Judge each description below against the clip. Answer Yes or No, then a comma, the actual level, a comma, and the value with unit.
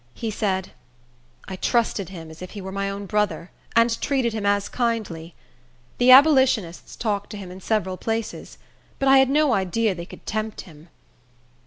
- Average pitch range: Yes, average, 3.7 semitones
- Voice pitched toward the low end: No, high, 210 Hz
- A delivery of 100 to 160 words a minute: No, average, 175 wpm